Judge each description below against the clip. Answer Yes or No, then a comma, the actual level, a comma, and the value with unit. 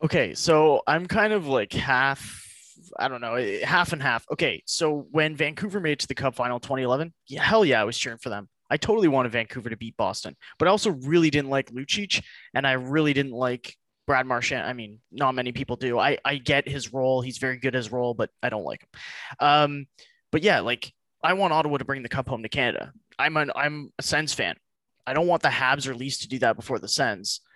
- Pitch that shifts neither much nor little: Yes, average, 3.4 semitones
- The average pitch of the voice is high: No, low, 135 Hz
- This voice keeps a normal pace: No, fast, 235 wpm